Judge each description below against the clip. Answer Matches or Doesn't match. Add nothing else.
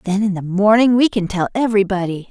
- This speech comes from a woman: Matches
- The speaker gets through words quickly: Matches